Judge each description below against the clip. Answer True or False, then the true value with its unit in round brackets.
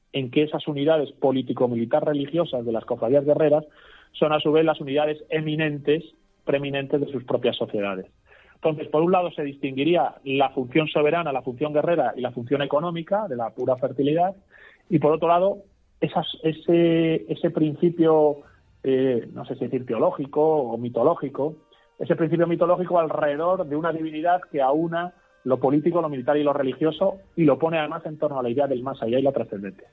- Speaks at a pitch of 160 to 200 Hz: False (150 Hz)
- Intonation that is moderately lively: True (3.3 semitones)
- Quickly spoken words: False (175 wpm)